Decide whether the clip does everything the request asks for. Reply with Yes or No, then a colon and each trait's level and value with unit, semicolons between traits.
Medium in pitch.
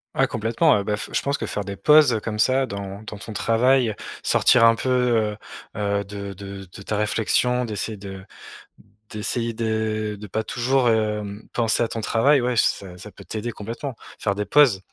No: low, 110 Hz